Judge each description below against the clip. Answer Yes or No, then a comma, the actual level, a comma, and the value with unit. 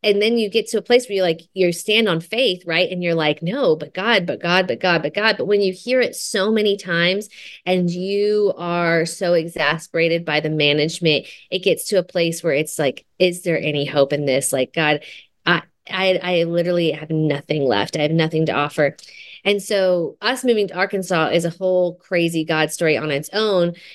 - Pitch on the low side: No, medium, 175 Hz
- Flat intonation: No, average, 3.5 semitones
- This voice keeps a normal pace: No, fast, 215 wpm